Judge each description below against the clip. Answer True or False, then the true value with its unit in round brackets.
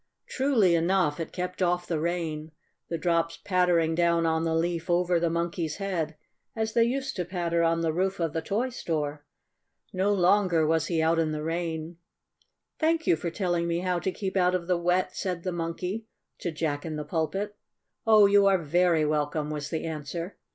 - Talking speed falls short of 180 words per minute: False (195 wpm)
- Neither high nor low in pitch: True (170 Hz)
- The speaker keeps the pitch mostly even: True (2.3 semitones)